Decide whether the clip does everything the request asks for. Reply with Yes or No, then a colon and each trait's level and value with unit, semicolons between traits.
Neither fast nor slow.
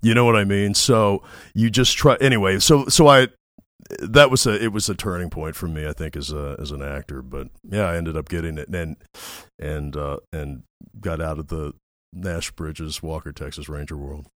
No: fast, 215 wpm